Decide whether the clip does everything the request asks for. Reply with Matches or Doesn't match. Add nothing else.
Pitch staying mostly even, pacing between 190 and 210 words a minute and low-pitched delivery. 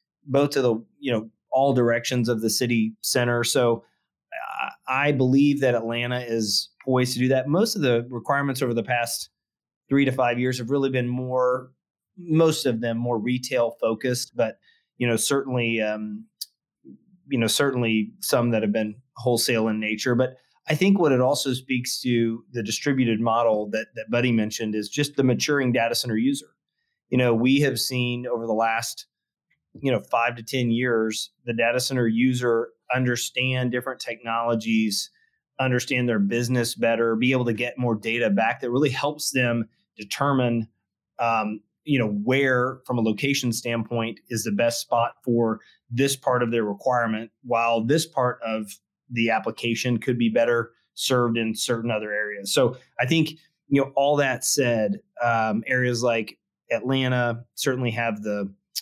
Doesn't match